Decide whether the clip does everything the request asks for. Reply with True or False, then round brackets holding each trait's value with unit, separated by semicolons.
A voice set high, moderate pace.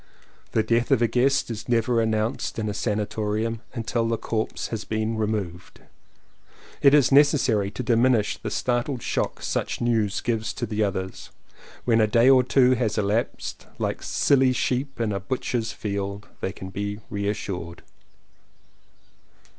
False (110 Hz; 155 wpm)